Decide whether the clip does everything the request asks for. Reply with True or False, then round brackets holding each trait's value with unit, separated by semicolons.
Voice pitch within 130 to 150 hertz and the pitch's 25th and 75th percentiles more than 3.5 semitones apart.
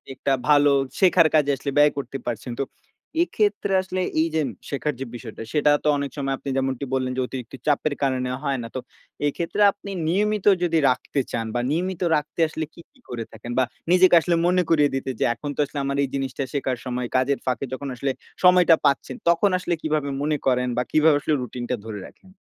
True (140 Hz; 4.2 semitones)